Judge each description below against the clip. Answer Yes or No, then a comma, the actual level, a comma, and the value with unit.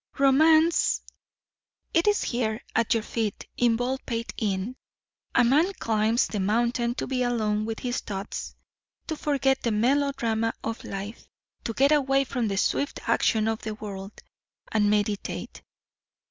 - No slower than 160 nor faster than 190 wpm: No, average, 145 wpm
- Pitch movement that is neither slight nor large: Yes, average, 3.9 semitones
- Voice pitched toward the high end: Yes, high, 230 Hz